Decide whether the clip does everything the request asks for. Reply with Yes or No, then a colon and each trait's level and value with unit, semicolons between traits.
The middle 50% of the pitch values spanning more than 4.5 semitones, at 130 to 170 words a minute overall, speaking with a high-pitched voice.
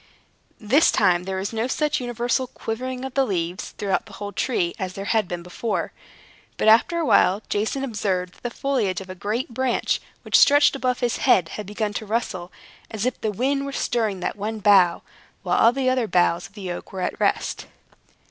No: average, 4.9 semitones; fast, 205 wpm; high, 220 Hz